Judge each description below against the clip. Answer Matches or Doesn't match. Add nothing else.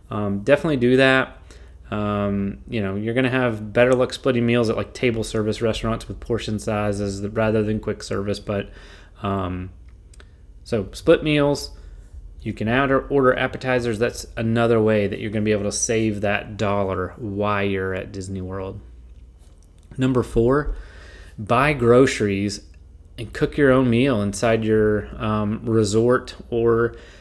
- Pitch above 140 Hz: Doesn't match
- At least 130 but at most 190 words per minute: Matches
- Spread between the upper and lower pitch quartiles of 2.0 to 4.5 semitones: Matches